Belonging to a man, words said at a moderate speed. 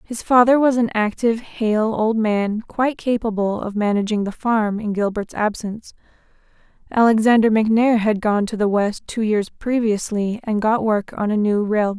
No: female; average, 170 wpm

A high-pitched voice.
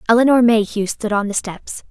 Yes: high, 220 Hz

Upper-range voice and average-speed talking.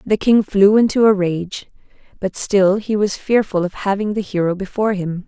Yes: high, 200 Hz; average, 195 wpm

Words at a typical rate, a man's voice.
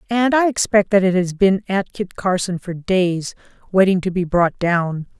No: average, 195 wpm; female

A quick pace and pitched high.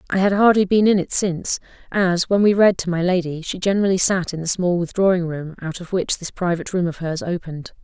No: fast, 240 wpm; medium, 180 Hz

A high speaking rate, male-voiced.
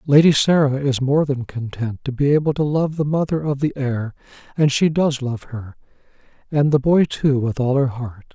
Yes: fast, 210 wpm; male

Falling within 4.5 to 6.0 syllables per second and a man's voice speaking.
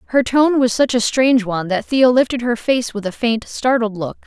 No: 5.3 syllables/s; female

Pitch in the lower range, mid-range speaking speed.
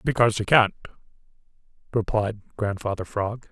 No: low, 105 Hz; slow, 100 wpm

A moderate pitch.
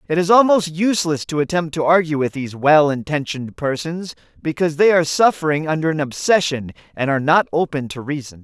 Yes: medium, 155 Hz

